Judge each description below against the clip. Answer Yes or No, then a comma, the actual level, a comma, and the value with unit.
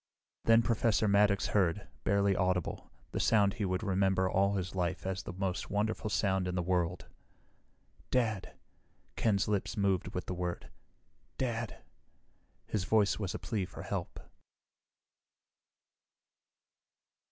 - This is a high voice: No, low, 100 Hz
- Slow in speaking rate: Yes, slow, 130 wpm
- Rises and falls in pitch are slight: Yes, narrow, 2.3 semitones